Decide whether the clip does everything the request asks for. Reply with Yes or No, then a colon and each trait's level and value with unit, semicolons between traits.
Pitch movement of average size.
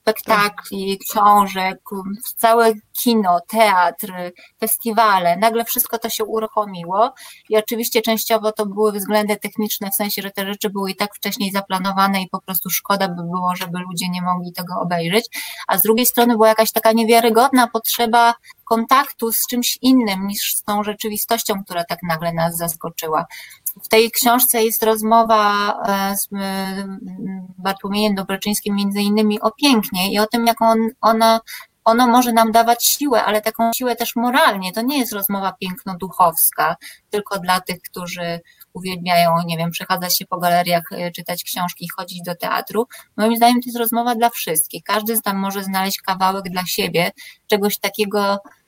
Yes: average, 3.2 semitones